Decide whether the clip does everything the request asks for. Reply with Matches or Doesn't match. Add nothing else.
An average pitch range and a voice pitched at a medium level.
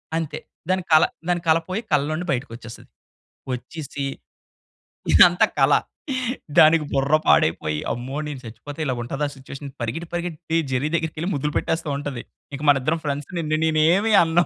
Matches